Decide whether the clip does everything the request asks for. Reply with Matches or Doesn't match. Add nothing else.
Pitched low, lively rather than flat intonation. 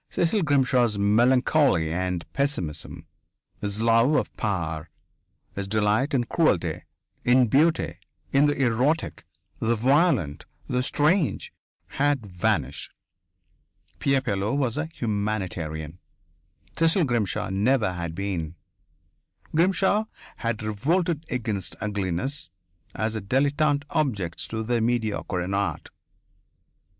Matches